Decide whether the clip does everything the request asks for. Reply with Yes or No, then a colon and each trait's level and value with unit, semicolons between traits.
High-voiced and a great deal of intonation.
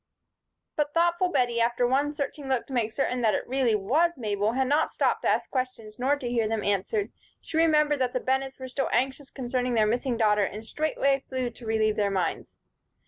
No: very high, 255 Hz; average, 3.9 semitones